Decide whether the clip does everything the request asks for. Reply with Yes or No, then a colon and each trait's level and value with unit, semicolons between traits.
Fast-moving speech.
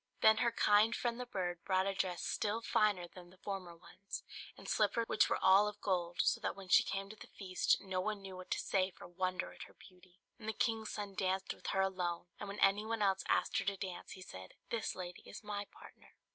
Yes: fast, 240 wpm